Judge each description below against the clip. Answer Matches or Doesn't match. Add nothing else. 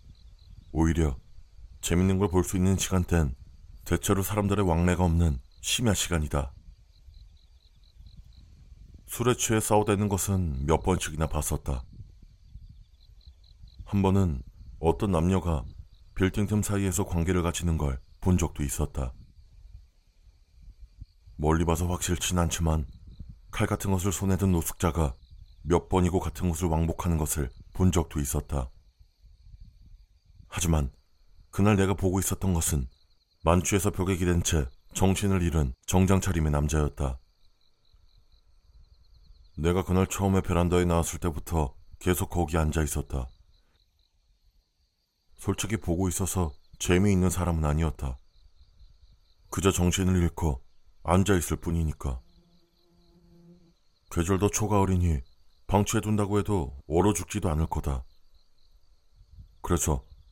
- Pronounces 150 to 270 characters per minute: Matches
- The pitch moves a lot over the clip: Doesn't match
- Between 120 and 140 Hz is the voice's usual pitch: Doesn't match